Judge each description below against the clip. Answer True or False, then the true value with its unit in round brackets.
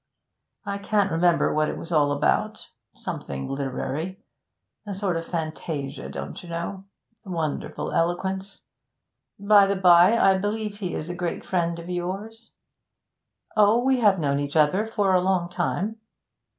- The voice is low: False (180 Hz)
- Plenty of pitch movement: False (3.4 semitones)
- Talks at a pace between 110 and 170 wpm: True (150 wpm)